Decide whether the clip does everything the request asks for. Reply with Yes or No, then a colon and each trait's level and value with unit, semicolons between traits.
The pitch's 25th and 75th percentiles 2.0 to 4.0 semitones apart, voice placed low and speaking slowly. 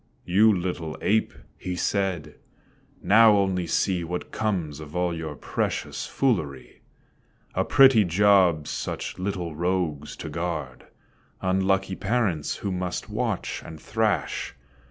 Yes: average, 3.3 semitones; very low, 90 Hz; slow, 120 wpm